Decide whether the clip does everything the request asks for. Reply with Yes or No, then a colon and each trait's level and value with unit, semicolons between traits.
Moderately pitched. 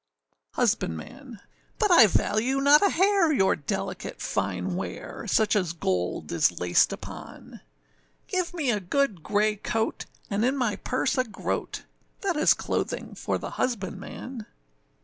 No: high, 220 Hz